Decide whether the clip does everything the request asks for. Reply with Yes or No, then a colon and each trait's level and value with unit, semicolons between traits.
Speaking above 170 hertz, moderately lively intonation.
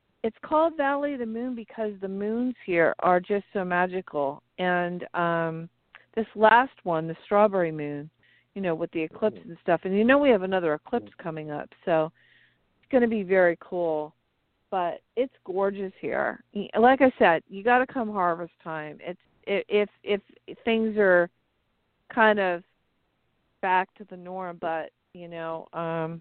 Yes: medium, 185 Hz; average, 4.8 semitones